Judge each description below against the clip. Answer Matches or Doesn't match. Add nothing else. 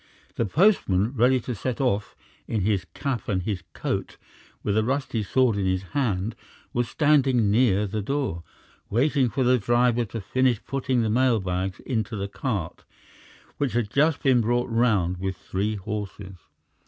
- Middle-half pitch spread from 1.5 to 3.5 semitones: Doesn't match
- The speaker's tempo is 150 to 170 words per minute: Matches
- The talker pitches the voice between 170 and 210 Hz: Doesn't match